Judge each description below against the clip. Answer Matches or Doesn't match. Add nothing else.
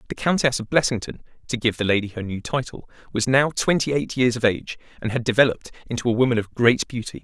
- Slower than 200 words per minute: Doesn't match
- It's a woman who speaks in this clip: Doesn't match